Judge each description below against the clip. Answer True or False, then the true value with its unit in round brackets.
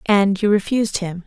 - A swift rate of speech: False (190 wpm)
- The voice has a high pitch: True (200 Hz)